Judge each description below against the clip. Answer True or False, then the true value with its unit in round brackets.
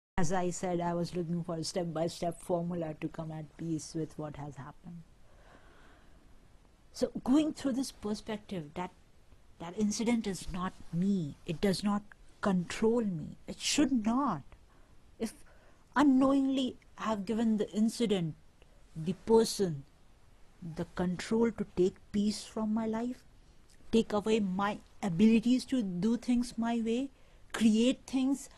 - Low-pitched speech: False (205 Hz)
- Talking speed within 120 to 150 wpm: True (140 wpm)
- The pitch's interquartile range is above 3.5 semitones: True (4.9 semitones)